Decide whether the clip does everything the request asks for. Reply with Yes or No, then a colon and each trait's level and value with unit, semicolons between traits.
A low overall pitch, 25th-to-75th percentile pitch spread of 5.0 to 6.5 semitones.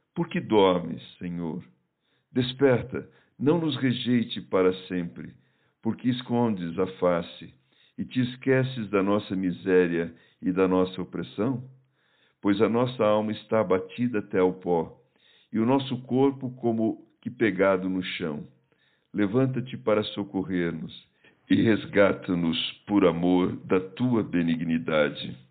Yes: low, 105 Hz; wide, 5.4 semitones